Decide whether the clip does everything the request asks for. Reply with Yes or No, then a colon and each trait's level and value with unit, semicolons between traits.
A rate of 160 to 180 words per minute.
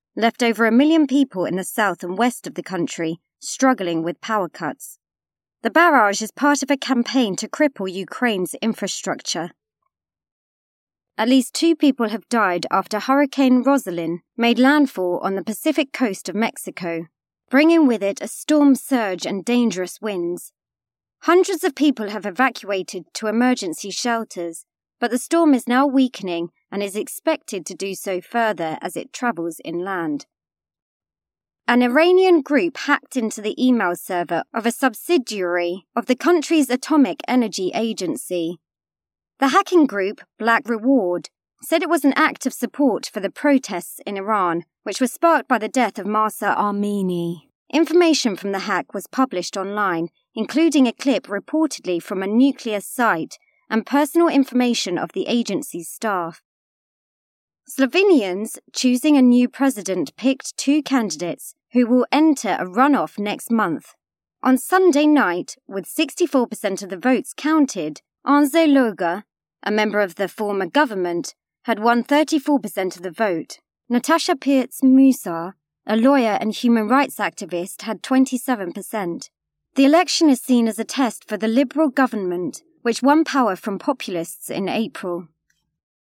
No: average, 145 wpm